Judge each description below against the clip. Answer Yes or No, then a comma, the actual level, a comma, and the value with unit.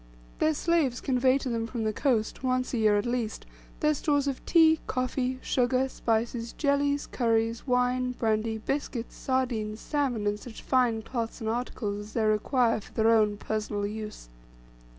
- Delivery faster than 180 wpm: No, average, 165 wpm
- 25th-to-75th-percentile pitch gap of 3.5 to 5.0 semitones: No, average, 3.0 semitones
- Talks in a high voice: Yes, high, 240 Hz